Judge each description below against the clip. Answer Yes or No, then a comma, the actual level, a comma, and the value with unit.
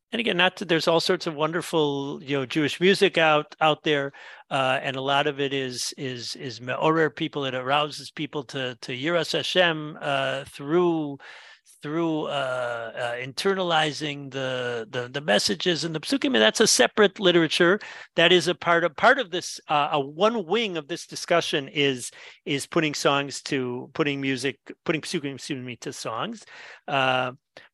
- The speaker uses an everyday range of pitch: Yes, average, 4.0 semitones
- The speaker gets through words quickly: No, average, 170 wpm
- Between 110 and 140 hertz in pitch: No, medium, 150 Hz